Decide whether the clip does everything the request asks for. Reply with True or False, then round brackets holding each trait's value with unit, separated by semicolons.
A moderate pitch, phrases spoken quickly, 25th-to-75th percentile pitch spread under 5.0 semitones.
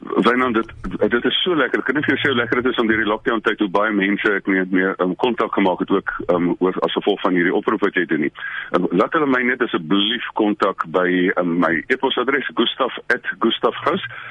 False (100 Hz; 245 wpm; 3.2 semitones)